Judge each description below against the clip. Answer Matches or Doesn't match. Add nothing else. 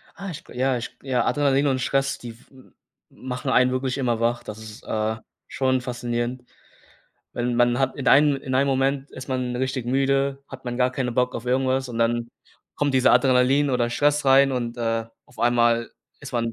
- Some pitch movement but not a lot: Doesn't match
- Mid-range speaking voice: Doesn't match